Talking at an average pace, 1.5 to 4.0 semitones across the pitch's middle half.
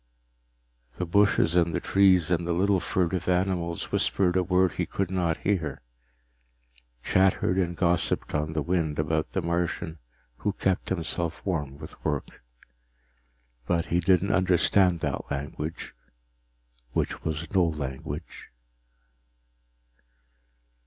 No: slow, 120 wpm; narrow, 2.6 semitones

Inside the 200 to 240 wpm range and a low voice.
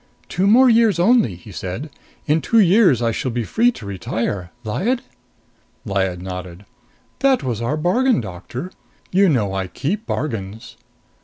No: average, 150 wpm; low, 130 Hz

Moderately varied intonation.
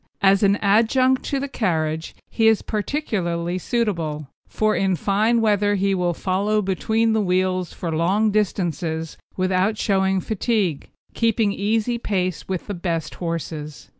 Yes: average, 3.7 semitones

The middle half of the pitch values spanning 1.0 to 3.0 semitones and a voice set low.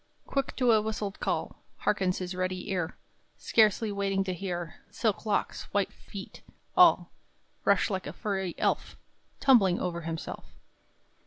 No: narrow, 2.5 semitones; high, 195 Hz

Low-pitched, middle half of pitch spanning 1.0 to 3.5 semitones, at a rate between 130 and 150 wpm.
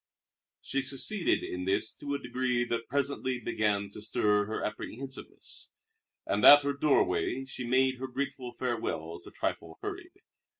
No: low, 125 Hz; average, 4.2 semitones; average, 145 wpm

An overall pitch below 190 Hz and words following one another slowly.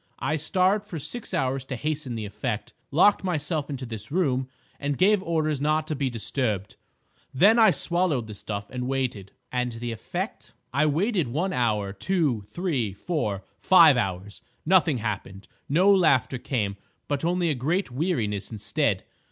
No: medium, 140 Hz; average, 160 wpm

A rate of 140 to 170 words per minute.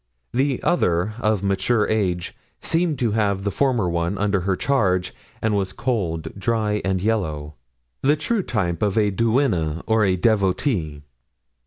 Yes: average, 145 wpm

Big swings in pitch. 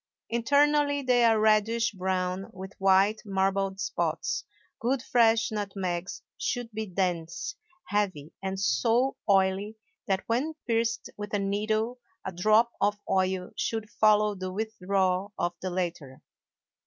No: average, 3.3 semitones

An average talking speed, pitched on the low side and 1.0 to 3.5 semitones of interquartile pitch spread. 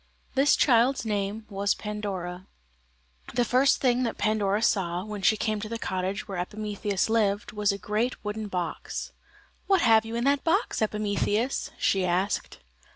No: average, 155 wpm; high, 210 Hz; narrow, 2.6 semitones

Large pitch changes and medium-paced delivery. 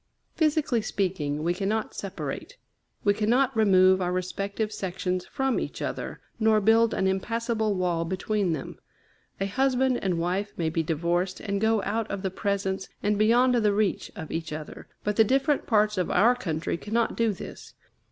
No: average, 3.5 semitones; average, 170 wpm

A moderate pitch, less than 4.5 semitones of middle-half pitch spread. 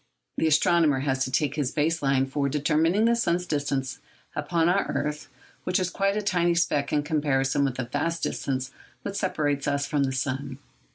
Yes: medium, 150 Hz; average, 3.7 semitones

